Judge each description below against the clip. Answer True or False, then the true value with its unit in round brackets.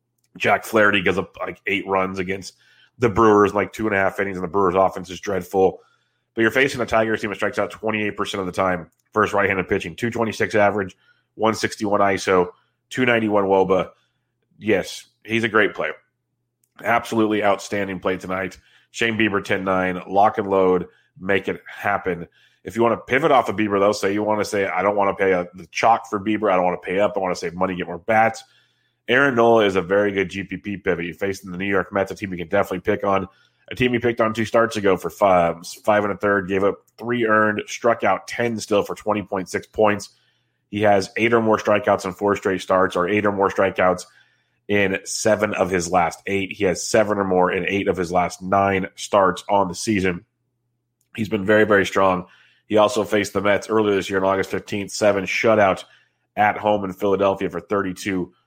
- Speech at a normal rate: False (215 wpm)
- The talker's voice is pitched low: True (100 Hz)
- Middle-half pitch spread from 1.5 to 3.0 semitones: True (2.5 semitones)